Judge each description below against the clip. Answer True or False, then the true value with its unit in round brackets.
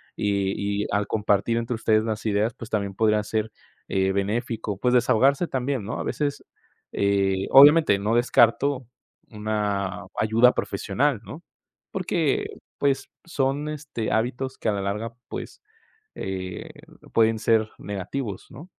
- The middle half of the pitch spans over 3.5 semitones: True (4.2 semitones)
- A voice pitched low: True (110 Hz)